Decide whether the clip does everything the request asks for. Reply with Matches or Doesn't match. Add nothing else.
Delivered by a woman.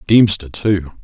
Doesn't match